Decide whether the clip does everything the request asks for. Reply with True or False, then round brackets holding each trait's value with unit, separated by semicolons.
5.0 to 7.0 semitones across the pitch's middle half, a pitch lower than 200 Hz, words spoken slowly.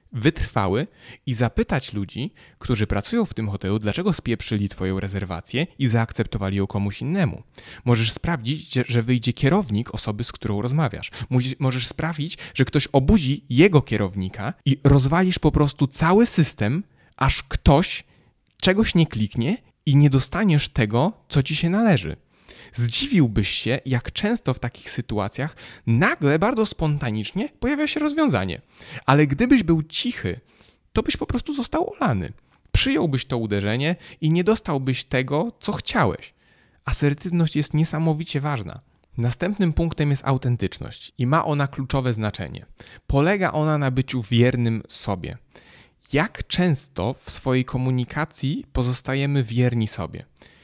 False (5.5 semitones; 135 Hz; 135 wpm)